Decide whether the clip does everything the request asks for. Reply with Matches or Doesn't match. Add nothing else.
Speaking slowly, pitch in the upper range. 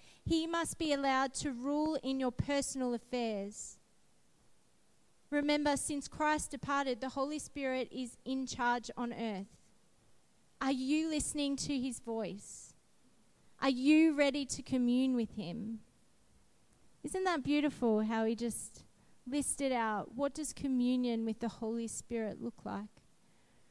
Matches